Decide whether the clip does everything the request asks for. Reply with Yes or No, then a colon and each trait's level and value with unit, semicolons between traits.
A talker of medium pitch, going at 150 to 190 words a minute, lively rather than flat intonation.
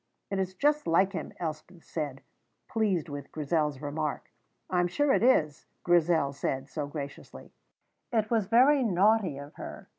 Yes: medium, 170 Hz; average, 155 wpm; wide, 6.3 semitones